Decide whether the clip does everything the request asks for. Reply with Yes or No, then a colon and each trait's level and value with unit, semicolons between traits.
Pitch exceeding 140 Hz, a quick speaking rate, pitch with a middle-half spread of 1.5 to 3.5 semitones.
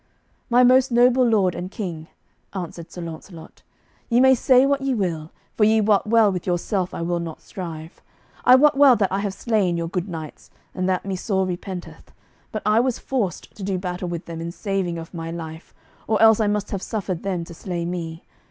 No: high, 190 Hz; fast, 210 wpm; average, 4.5 semitones